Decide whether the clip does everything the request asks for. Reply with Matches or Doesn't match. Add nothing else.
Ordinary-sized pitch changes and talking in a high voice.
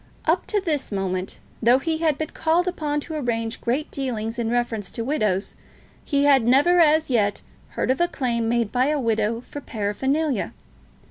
Matches